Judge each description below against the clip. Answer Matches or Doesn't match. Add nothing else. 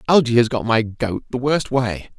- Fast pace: Matches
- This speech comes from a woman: Doesn't match